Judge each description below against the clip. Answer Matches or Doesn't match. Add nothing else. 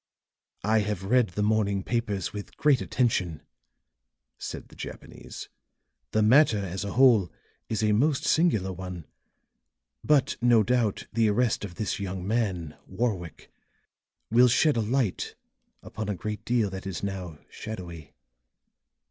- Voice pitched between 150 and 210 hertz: Doesn't match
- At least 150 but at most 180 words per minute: Doesn't match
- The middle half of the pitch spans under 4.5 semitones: Matches